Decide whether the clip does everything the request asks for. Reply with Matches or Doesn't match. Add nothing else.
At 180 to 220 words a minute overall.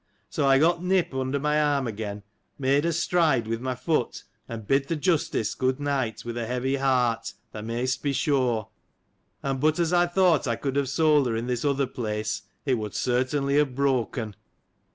Matches